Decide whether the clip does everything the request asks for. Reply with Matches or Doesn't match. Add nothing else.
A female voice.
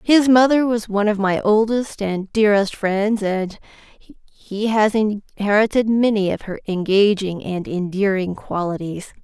Matches